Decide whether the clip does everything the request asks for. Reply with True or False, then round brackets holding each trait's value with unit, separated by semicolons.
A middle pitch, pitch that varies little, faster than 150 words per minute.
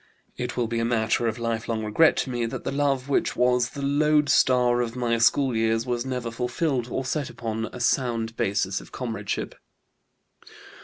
False (120 Hz; 2.2 semitones; 175 wpm)